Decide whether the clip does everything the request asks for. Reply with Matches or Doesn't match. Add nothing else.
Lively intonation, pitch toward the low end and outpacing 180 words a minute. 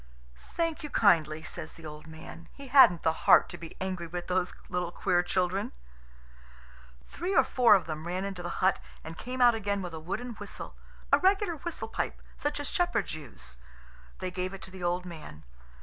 Doesn't match